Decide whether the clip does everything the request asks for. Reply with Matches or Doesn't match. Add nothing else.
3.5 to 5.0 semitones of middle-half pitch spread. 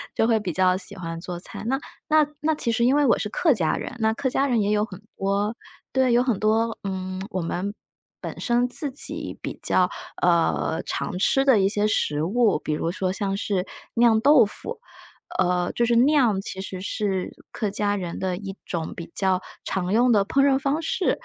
Matches